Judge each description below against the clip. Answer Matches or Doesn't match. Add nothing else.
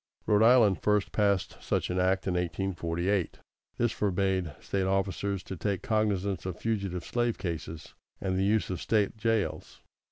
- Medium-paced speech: Matches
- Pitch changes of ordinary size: Doesn't match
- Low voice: Matches